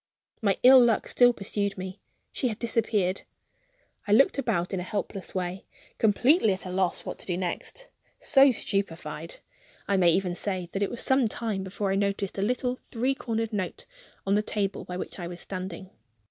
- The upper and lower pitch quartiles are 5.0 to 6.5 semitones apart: No, average, 3.8 semitones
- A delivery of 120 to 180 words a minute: No, average, 190 wpm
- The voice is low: No, high, 200 Hz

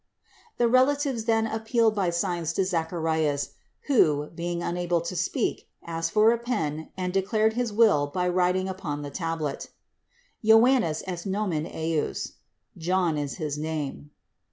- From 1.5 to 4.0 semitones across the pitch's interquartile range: No, wide, 5.4 semitones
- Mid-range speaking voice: Yes, medium, 180 Hz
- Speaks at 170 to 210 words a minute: No, average, 150 wpm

